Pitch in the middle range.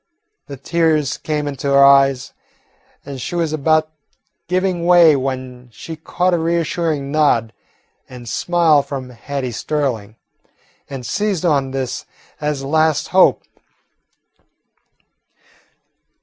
Yes: medium, 145 Hz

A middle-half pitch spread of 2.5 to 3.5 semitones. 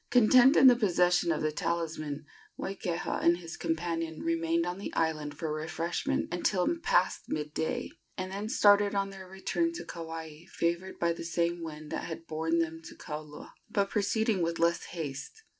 Yes: average, 3.1 semitones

